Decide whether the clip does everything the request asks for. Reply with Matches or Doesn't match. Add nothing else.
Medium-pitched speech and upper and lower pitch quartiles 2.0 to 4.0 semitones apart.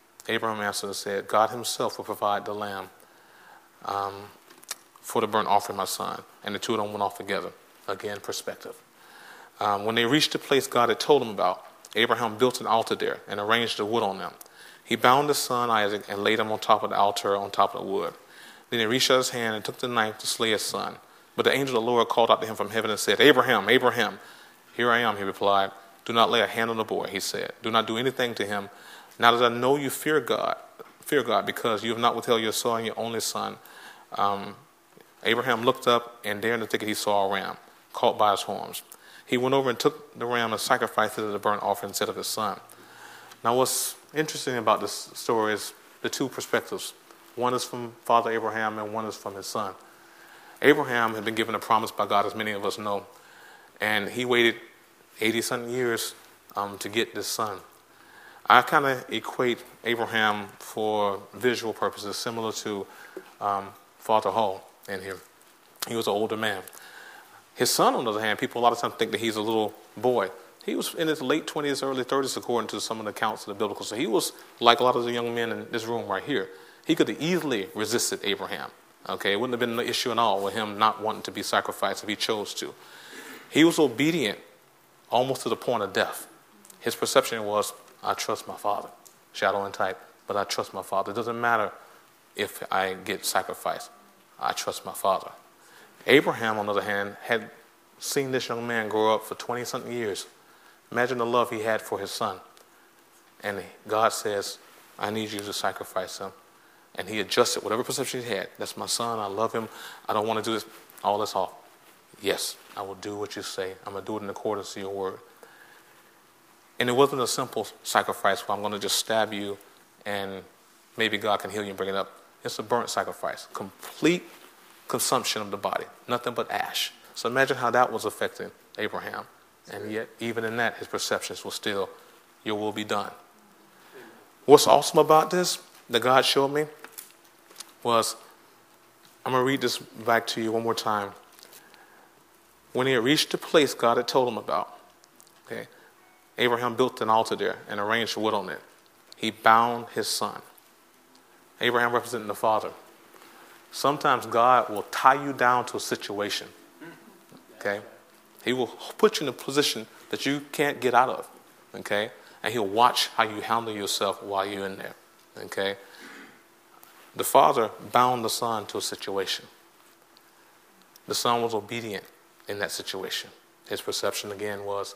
Doesn't match